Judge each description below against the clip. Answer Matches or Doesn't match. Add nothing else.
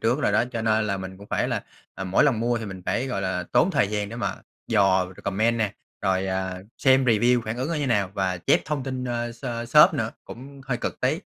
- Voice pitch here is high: Doesn't match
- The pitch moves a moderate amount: Matches